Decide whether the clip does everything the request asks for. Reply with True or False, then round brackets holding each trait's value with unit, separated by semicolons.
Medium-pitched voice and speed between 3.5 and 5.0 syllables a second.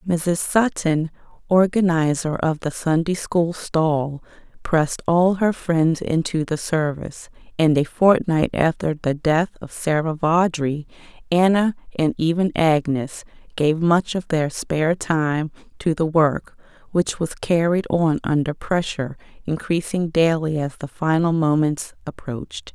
True (160 Hz; 4.0 syllables/s)